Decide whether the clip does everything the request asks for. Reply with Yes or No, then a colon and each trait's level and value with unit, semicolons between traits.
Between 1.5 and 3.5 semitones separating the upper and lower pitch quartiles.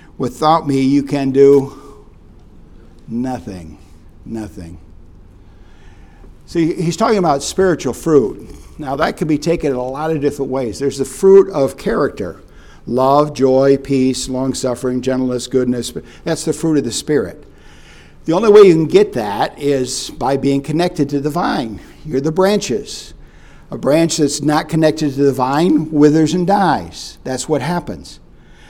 No: wide, 5.5 semitones